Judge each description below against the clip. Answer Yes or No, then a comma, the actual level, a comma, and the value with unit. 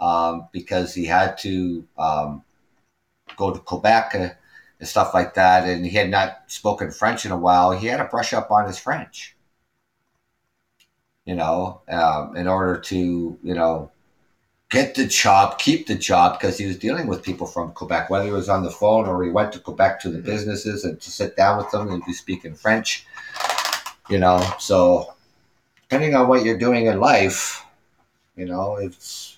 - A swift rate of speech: No, average, 185 wpm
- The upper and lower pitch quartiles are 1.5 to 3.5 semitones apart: Yes, average, 2.8 semitones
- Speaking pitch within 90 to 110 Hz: Yes, very low, 95 Hz